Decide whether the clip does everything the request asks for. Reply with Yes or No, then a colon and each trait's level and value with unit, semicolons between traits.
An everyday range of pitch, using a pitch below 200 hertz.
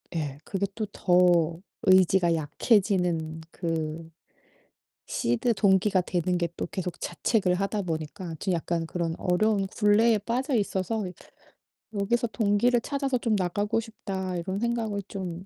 Yes: average, 3.9 semitones; high, 190 Hz